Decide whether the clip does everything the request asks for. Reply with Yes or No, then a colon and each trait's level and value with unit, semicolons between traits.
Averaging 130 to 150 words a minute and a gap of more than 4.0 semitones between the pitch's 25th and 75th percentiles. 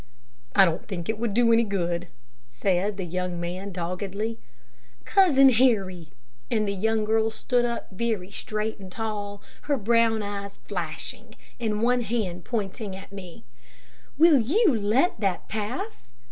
No: average, 145 wpm; average, 3.6 semitones